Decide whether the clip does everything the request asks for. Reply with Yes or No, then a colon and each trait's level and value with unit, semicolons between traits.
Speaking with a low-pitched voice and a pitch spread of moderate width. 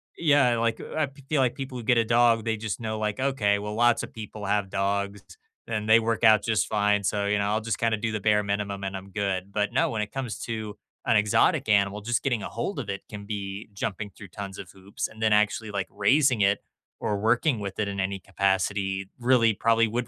No: low, 105 Hz; narrow, 2.3 semitones